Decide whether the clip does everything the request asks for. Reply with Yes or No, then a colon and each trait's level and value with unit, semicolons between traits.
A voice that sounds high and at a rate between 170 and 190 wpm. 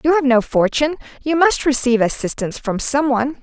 Yes: very high, 265 Hz; average, 175 wpm